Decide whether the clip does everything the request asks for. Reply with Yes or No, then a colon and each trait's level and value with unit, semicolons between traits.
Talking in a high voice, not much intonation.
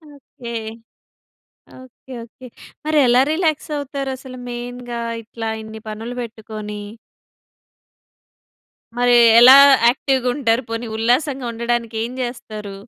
Yes: high, 240 Hz; narrow, 2.3 semitones